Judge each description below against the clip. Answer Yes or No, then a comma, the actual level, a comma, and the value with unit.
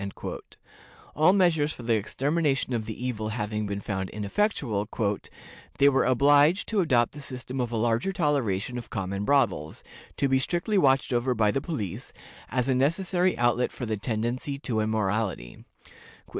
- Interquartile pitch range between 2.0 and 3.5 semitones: No, average, 4.9 semitones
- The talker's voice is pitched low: Yes, low, 125 Hz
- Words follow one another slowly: No, average, 155 wpm